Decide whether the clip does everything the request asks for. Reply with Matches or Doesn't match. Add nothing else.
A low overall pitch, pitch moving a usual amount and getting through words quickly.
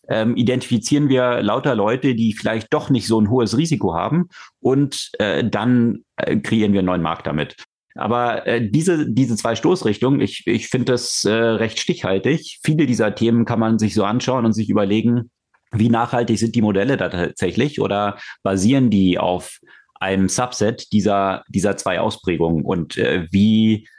Doesn't match